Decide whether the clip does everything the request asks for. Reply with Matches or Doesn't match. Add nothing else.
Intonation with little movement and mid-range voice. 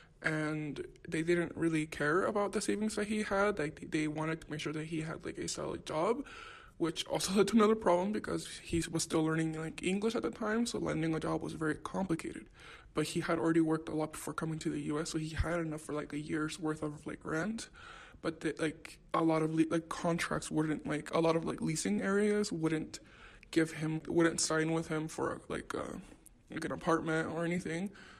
Matches